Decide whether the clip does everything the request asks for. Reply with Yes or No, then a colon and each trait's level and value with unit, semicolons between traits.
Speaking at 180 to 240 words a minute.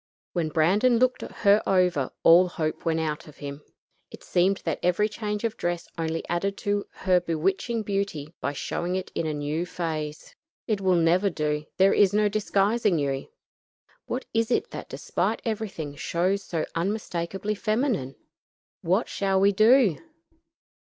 No: average, 155 wpm